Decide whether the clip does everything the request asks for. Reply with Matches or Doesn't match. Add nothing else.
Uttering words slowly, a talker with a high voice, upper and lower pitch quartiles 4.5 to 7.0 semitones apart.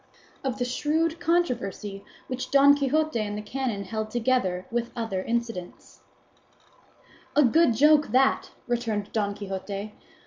Matches